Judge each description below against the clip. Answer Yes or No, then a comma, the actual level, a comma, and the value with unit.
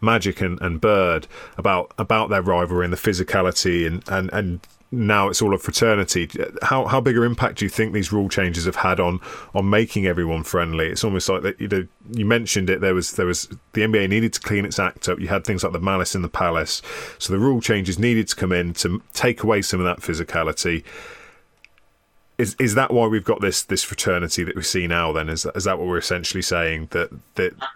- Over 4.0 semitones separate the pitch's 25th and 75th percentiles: No, average, 3.5 semitones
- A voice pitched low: Yes, very low, 95 Hz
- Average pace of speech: No, fast, 225 wpm